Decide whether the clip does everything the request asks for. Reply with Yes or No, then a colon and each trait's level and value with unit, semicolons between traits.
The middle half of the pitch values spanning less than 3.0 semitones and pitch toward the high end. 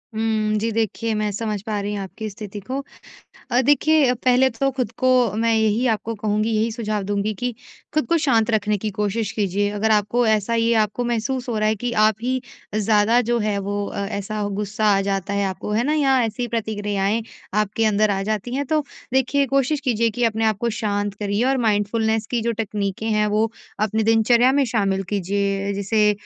Yes: narrow, 2.4 semitones; high, 220 Hz